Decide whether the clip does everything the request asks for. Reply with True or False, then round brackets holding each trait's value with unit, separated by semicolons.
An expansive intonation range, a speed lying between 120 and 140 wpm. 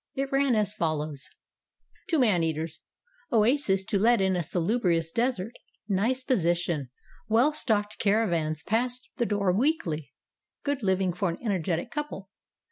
True (5.8 semitones; 135 wpm)